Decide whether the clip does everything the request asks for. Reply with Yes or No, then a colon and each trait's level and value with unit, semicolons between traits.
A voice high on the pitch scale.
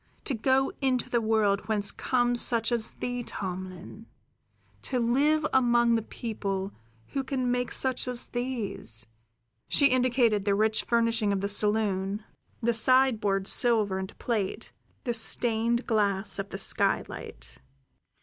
Yes: high, 230 Hz